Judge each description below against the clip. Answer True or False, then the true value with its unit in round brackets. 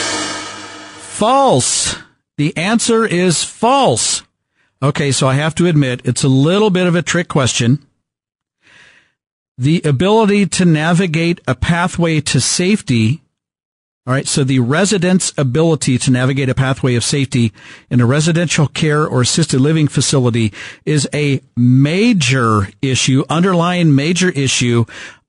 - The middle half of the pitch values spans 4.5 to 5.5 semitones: True (4.8 semitones)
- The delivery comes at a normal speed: False (130 wpm)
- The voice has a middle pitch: True (145 Hz)